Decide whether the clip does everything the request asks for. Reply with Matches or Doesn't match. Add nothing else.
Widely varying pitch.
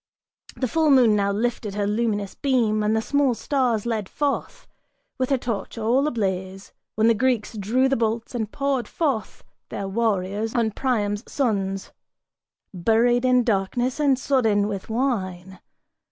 Doesn't match